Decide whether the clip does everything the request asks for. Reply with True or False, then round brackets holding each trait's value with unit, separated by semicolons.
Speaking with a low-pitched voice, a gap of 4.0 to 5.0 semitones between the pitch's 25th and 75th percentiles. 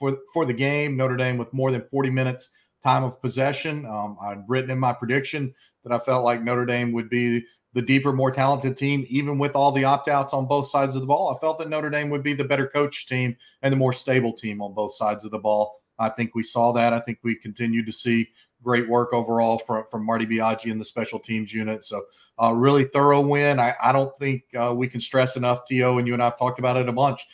False (125 Hz; 2.9 semitones)